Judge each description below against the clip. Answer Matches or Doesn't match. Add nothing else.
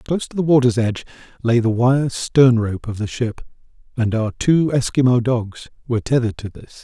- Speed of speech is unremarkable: Matches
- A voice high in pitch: Doesn't match